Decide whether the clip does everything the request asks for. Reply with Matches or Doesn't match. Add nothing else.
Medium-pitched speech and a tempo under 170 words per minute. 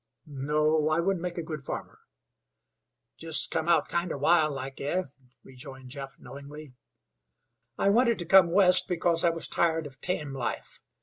Matches